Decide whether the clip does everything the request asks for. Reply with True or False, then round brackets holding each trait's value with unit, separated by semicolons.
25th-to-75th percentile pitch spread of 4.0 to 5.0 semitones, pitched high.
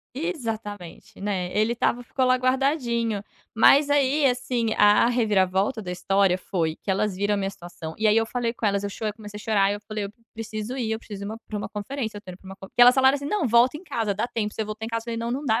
False (3.3 semitones; 220 Hz)